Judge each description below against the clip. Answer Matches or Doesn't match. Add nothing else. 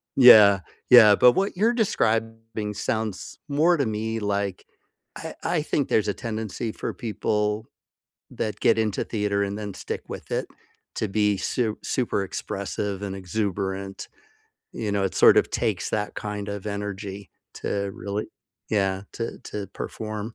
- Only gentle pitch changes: Matches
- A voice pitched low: Matches